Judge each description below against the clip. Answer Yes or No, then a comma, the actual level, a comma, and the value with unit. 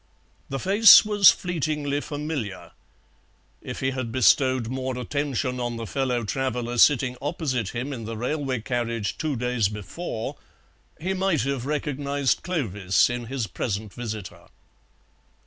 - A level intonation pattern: No, average, 3.8 semitones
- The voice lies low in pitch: Yes, low, 130 Hz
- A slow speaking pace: Yes, slow, 130 wpm